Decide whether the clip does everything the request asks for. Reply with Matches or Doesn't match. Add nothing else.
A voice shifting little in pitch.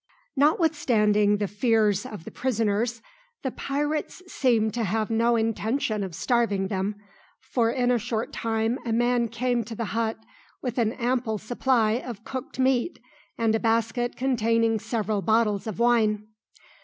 Matches